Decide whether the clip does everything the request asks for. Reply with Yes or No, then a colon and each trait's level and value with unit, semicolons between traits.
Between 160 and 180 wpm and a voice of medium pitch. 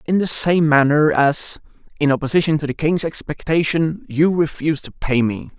Yes: average, 170 wpm; medium, 150 Hz